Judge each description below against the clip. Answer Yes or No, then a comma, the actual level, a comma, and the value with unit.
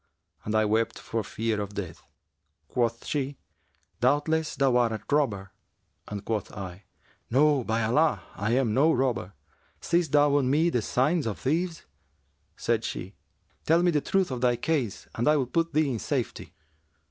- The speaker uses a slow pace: No, average, 170 wpm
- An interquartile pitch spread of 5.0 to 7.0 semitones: Yes, average, 5.3 semitones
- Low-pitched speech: Yes, low, 125 Hz